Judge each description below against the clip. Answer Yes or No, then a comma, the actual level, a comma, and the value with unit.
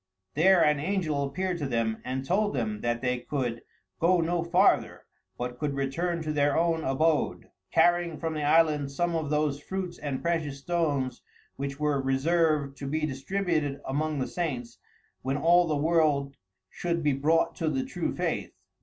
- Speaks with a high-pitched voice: No, medium, 150 Hz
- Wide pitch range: No, average, 3.6 semitones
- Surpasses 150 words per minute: Yes, average, 170 wpm